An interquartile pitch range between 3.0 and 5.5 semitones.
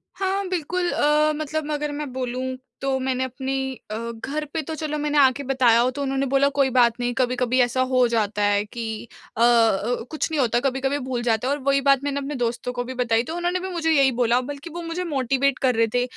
Yes: average, 3.4 semitones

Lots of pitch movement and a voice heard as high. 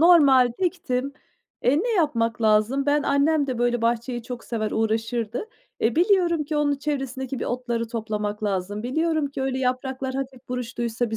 No: average, 3.7 semitones; very high, 255 Hz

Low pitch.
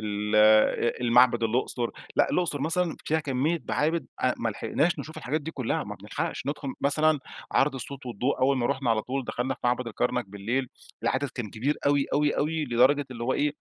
Yes: low, 130 Hz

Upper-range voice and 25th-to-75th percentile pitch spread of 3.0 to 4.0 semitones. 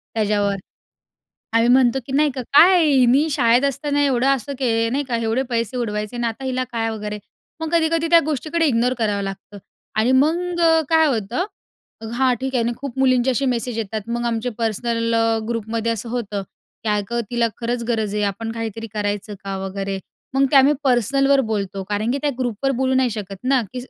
Yes: high, 240 Hz; average, 3.4 semitones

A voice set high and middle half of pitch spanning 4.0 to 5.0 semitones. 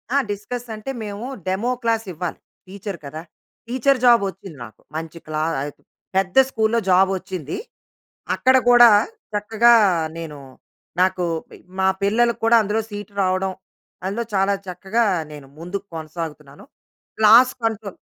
Yes: high, 200 Hz; average, 4.3 semitones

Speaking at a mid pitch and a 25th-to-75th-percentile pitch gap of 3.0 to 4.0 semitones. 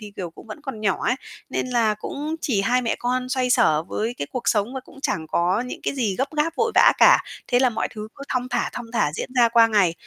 No: high, 235 Hz; average, 3.4 semitones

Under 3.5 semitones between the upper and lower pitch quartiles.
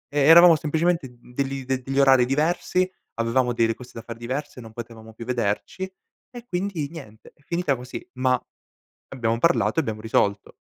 No: average, 5.2 semitones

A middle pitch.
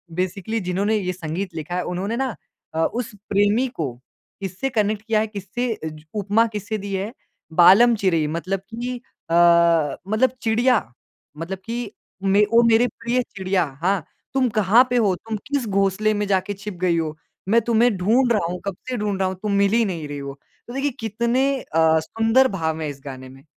No: high, 200 Hz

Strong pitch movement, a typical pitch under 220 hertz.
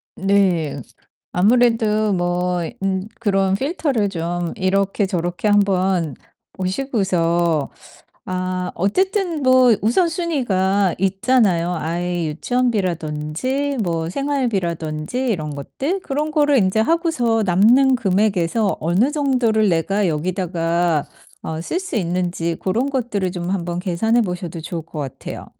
Yes: wide, 5.8 semitones; high, 195 Hz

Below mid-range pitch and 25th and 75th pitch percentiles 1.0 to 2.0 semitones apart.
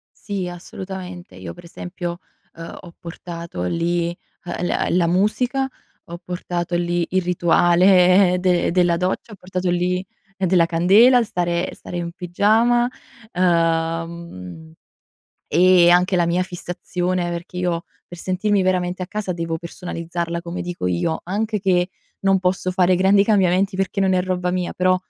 No: medium, 180 Hz; narrow, 1.5 semitones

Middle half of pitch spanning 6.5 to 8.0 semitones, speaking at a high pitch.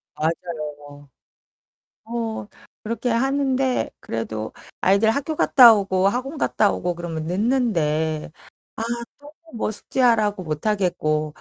Yes: wide, 7.1 semitones; high, 200 Hz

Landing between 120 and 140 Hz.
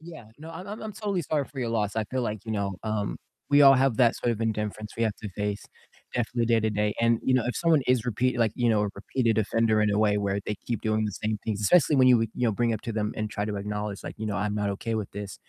No: low, 110 Hz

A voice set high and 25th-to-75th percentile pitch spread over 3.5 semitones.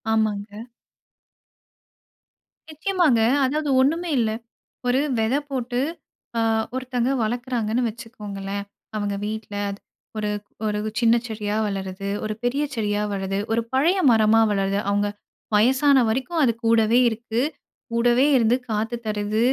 No: high, 225 Hz; average, 3.2 semitones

